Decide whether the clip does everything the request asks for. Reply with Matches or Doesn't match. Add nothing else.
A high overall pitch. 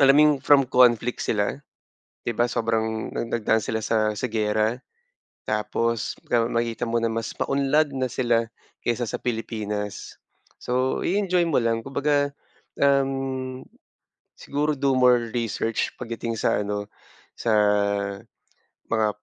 Doesn't match